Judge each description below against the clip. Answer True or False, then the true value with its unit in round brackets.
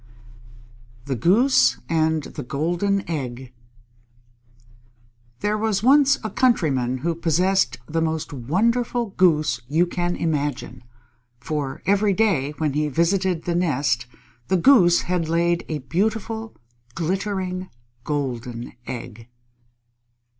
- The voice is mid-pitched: True (165 Hz)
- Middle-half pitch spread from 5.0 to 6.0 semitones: True (5.5 semitones)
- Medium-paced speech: False (110 wpm)